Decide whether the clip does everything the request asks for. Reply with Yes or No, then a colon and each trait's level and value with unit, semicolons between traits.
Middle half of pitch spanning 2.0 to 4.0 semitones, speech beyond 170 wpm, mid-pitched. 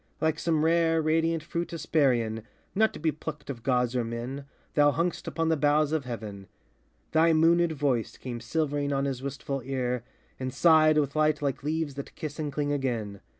Yes: average, 3.6 semitones; average, 185 wpm; medium, 145 Hz